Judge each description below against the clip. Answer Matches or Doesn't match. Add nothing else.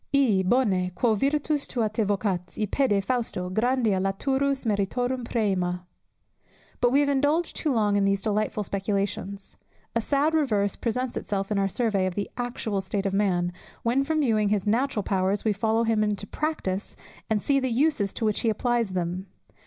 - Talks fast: Doesn't match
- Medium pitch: Doesn't match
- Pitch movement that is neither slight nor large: Matches